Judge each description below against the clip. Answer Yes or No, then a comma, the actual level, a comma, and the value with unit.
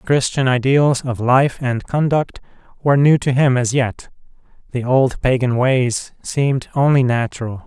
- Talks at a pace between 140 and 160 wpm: Yes, average, 155 wpm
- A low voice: Yes, low, 130 Hz